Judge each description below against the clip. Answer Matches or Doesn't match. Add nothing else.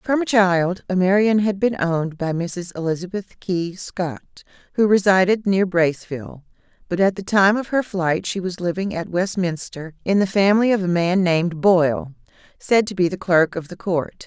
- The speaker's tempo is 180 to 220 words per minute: Matches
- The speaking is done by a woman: Matches